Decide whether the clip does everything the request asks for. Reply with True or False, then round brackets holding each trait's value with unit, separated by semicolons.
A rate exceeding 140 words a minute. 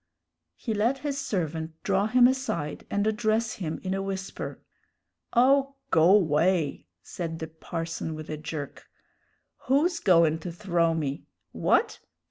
False (135 wpm)